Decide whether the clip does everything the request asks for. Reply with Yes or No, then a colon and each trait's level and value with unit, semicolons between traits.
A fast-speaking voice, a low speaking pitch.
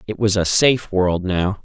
Yes: fast, 220 wpm; low, 100 Hz